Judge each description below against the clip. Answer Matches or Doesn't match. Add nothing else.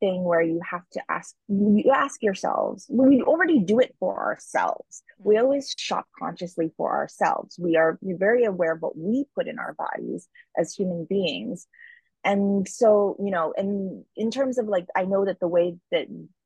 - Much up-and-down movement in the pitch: Matches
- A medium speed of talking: Matches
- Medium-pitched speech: Doesn't match